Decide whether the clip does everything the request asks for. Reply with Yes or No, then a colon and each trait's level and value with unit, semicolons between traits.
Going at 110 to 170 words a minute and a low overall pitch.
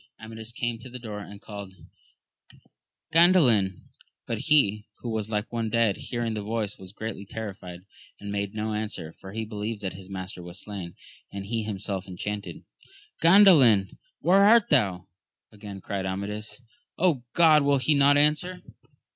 Yes: average, 155 wpm; low, 105 Hz